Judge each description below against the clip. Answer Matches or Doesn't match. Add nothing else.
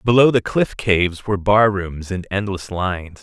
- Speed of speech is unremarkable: Matches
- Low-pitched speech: Matches